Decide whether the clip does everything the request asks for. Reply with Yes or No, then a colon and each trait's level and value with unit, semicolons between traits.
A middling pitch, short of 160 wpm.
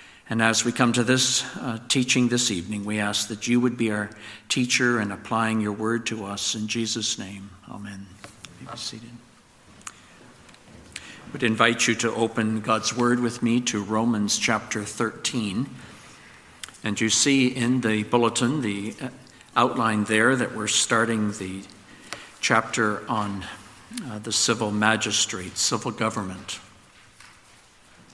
No: low, 110 Hz; average, 140 wpm